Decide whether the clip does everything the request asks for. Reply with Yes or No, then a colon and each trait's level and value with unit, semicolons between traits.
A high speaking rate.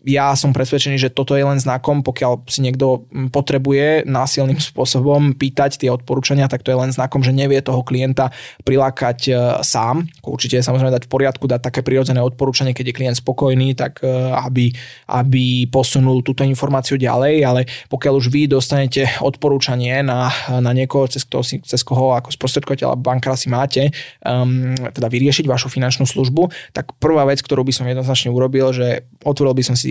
Yes: fast, 175 wpm